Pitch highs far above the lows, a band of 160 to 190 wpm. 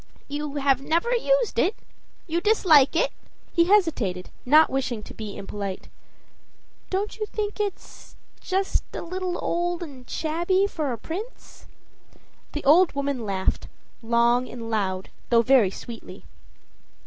No: wide, 7.8 semitones; slow, 135 wpm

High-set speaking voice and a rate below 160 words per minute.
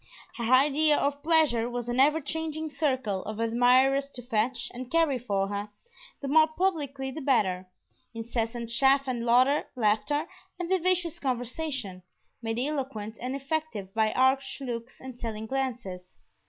Yes: very high, 255 Hz; average, 140 wpm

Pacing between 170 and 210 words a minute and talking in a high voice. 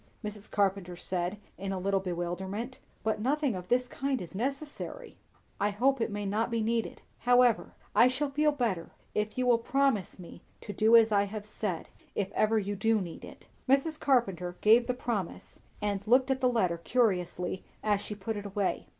Yes: average, 185 wpm; high, 215 Hz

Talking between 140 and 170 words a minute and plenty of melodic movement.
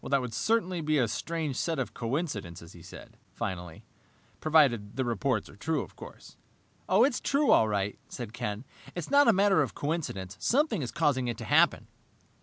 No: average, 180 wpm; wide, 8.0 semitones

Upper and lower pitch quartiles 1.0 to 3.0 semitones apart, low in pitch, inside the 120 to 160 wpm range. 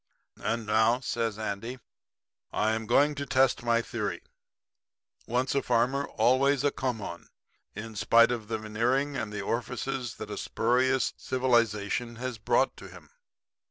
Yes: average, 2.7 semitones; low, 120 Hz; average, 150 wpm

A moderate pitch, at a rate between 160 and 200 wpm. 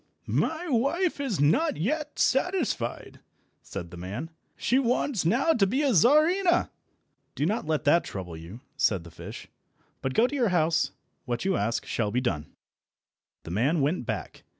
Yes: medium, 175 Hz; average, 165 wpm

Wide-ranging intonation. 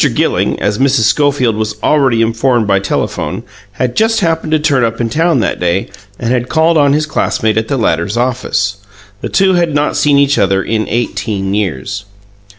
Yes: wide, 5.7 semitones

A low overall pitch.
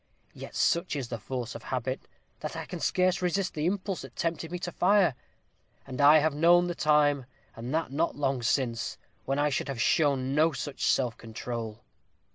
No: medium, 145 Hz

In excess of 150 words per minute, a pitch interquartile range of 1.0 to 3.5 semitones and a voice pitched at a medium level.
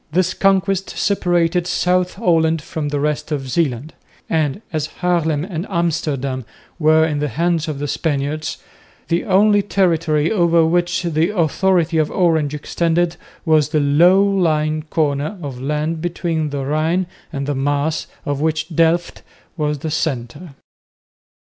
No: average, 145 wpm; average, 2.8 semitones; medium, 160 Hz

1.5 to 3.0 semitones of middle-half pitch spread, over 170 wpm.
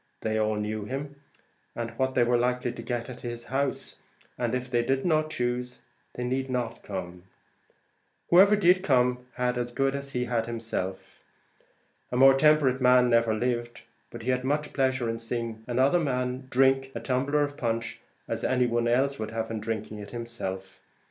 Yes: narrow, 2.4 semitones; average, 180 wpm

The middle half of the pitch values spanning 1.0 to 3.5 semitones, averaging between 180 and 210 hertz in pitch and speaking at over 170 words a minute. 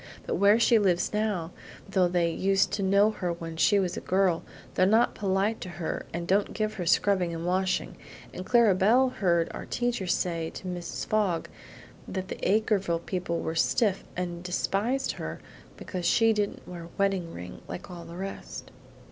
Yes: average, 3.0 semitones; medium, 185 Hz; average, 180 wpm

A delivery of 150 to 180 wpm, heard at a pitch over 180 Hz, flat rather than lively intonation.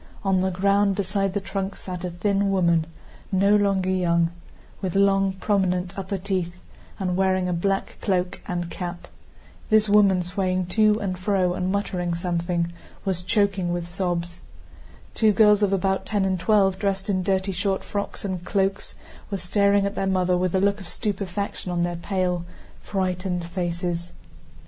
Yes: average, 165 wpm; high, 190 Hz; narrow, 1.9 semitones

